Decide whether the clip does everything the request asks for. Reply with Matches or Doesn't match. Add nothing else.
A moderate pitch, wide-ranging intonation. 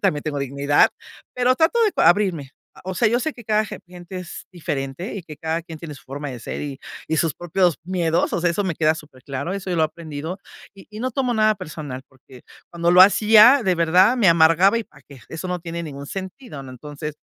Doesn't match